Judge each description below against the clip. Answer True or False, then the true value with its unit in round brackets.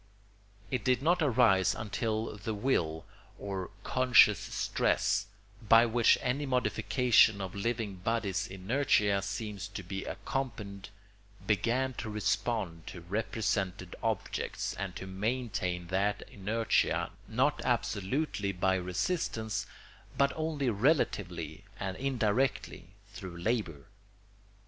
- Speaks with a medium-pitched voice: False (105 Hz)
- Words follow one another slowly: True (105 wpm)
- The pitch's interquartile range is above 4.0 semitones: True (4.4 semitones)